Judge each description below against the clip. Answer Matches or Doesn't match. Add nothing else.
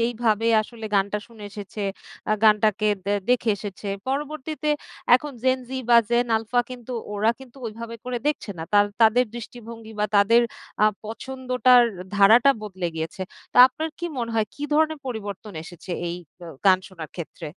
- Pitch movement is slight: Doesn't match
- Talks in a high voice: Matches